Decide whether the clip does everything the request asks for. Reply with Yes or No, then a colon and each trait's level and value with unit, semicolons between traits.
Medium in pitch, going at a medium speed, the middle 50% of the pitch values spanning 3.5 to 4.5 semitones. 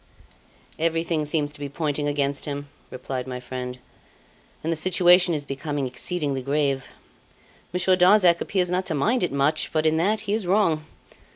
Yes: medium, 155 Hz; average, 165 wpm; average, 4.0 semitones